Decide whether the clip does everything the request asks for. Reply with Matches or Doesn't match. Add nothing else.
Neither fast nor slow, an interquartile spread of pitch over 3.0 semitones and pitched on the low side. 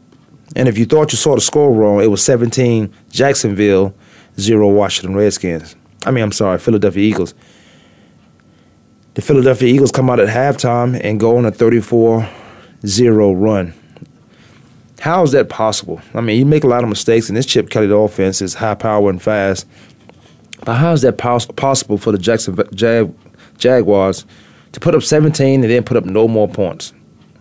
Matches